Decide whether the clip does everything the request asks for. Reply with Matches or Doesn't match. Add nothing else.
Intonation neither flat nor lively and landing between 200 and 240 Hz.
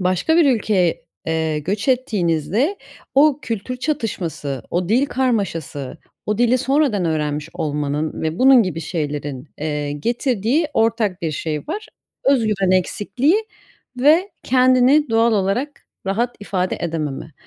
Doesn't match